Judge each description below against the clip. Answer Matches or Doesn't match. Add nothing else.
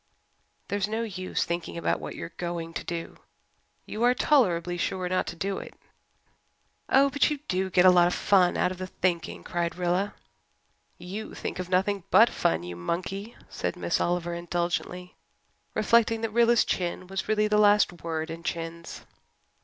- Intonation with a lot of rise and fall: Doesn't match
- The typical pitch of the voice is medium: Matches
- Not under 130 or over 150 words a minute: Doesn't match